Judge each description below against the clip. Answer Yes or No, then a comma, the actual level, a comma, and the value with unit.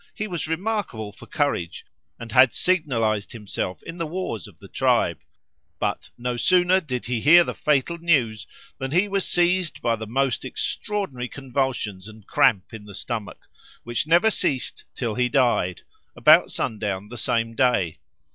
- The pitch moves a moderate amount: No, wide, 7.2 semitones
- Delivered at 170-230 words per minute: No, average, 160 wpm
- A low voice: Yes, low, 125 Hz